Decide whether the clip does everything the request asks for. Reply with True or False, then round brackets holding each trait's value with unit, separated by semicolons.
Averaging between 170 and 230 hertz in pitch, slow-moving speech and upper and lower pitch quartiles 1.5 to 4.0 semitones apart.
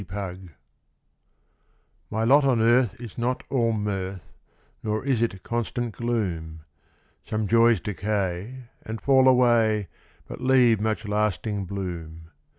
False (110 Hz; 125 wpm; 3.6 semitones)